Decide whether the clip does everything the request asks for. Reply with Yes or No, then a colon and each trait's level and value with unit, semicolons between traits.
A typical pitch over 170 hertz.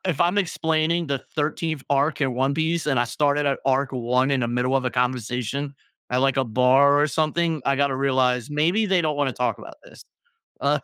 No: medium, 140 Hz